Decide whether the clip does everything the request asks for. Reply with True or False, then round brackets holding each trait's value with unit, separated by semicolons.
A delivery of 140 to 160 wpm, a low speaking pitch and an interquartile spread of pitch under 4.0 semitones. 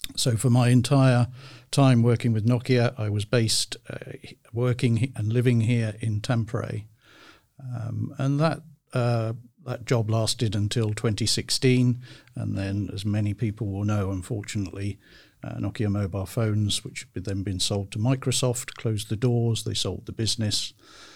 True (150 wpm; 115 Hz; 2.8 semitones)